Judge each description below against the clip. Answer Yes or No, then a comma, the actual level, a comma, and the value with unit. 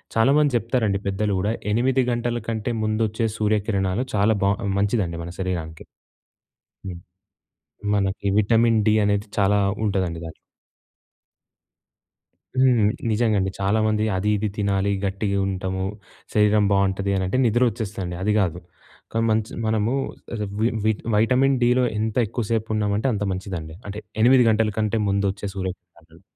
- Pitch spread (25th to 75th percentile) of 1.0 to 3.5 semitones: Yes, narrow, 2.5 semitones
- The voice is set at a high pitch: No, low, 105 Hz